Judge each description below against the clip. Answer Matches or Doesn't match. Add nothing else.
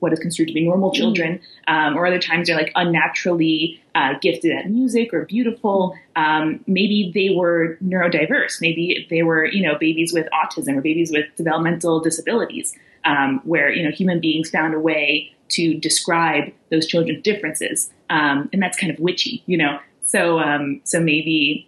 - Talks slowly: Doesn't match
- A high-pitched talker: Doesn't match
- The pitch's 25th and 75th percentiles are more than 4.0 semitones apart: Doesn't match